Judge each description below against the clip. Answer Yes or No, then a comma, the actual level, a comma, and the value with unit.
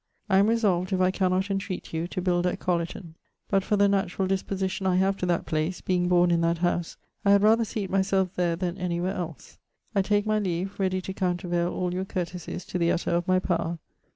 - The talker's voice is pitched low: No, medium, 185 Hz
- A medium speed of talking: No, fast, 225 wpm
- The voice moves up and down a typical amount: No, narrow, 1.8 semitones